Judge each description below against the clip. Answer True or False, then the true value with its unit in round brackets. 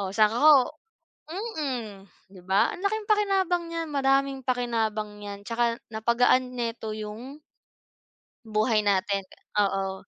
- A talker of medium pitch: False (235 Hz)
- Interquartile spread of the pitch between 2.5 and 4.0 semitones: False (4.5 semitones)